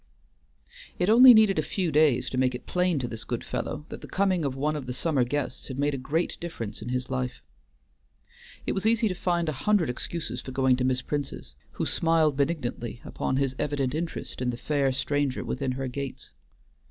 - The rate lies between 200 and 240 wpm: Yes, fast, 205 wpm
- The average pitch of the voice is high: No, medium, 140 Hz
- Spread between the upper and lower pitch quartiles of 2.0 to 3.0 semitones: No, average, 4.5 semitones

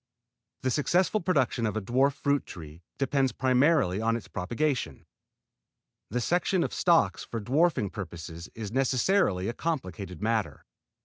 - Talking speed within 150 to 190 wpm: No, slow, 135 wpm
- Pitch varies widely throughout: Yes, wide, 6.4 semitones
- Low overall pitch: Yes, low, 120 Hz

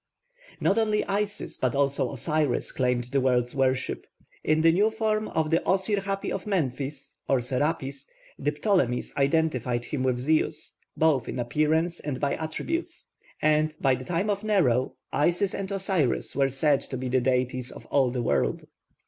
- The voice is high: No, medium, 145 Hz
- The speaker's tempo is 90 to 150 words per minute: No, average, 165 wpm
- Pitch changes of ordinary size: No, wide, 5.9 semitones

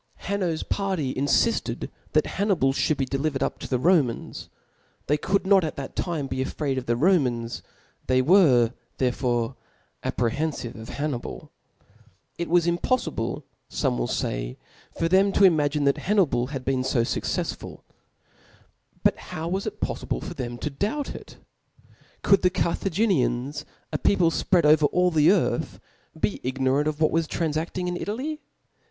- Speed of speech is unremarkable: Yes, average, 155 wpm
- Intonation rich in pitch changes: Yes, wide, 5.7 semitones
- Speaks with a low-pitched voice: No, medium, 150 Hz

